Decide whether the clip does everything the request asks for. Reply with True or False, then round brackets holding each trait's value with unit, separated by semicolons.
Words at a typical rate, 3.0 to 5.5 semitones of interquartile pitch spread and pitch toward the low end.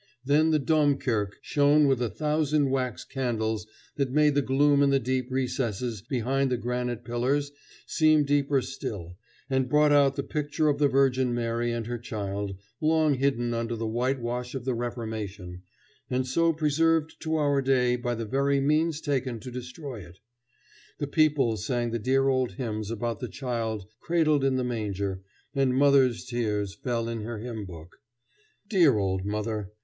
True (165 wpm; 3.6 semitones; 125 Hz)